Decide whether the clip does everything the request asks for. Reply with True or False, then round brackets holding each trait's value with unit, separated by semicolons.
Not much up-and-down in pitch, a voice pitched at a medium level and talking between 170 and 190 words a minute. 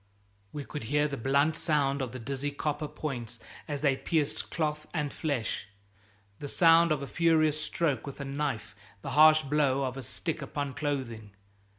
True (2.2 semitones; 145 Hz; 175 wpm)